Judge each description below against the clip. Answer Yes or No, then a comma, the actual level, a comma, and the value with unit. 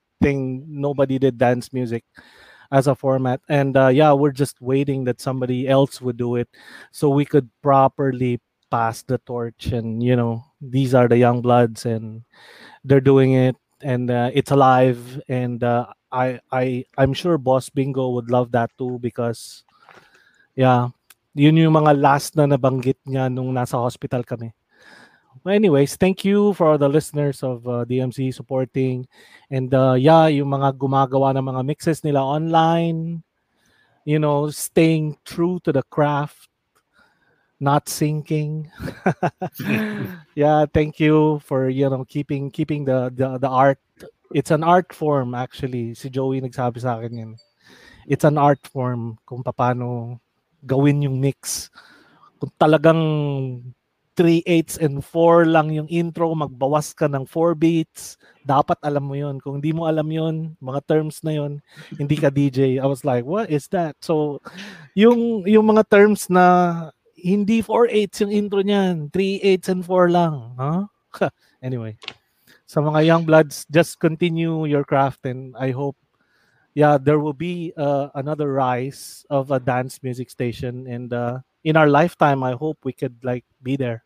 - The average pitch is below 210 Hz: Yes, medium, 140 Hz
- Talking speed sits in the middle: No, fast, 160 wpm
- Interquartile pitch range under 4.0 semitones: Yes, average, 3.5 semitones